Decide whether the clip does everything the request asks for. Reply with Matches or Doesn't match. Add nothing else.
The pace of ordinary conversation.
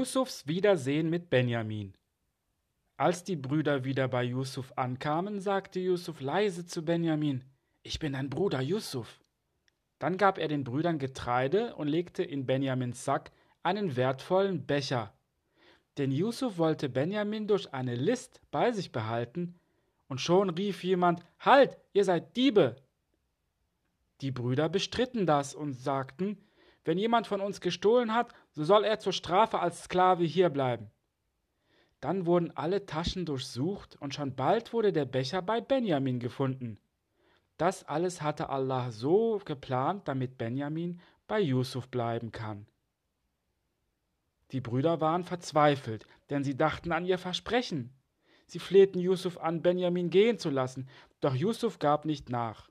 Matches